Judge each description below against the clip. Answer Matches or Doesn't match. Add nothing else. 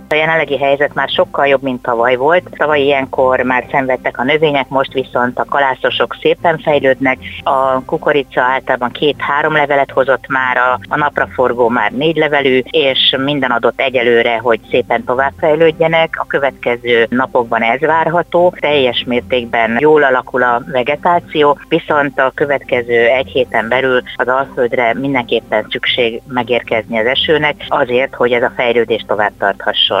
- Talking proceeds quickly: Doesn't match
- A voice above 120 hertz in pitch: Matches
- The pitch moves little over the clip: Doesn't match